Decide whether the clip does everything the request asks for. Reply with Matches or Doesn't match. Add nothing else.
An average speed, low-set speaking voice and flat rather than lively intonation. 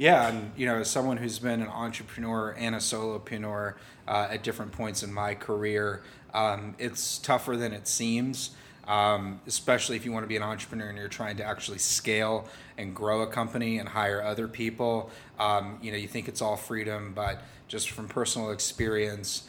Matches